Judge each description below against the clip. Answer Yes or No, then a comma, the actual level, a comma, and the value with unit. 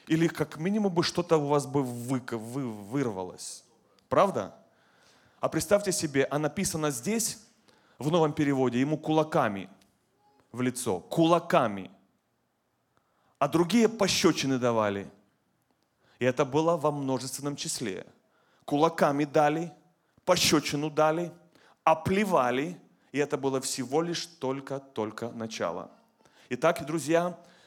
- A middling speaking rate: No, slow, 105 wpm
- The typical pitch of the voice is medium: Yes, medium, 150 Hz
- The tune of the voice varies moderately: Yes, average, 4.2 semitones